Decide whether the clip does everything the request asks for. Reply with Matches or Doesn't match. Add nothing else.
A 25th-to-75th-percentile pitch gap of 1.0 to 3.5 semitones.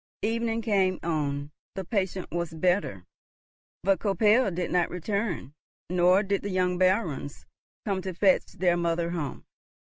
Matches